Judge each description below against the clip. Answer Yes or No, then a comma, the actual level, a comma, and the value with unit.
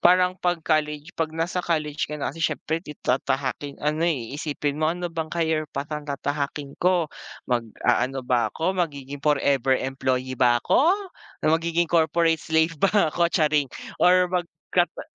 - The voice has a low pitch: No, medium, 155 Hz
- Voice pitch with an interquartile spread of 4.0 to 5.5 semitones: No, average, 3.2 semitones